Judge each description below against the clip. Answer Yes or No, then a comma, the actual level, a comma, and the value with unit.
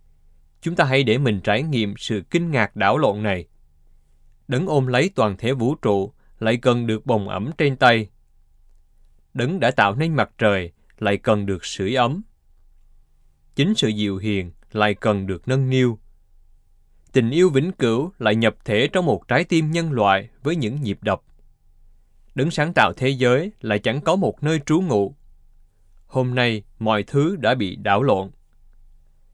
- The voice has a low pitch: Yes, low, 110 Hz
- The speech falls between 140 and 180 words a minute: Yes, average, 170 wpm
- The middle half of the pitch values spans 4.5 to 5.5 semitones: Yes, average, 5.2 semitones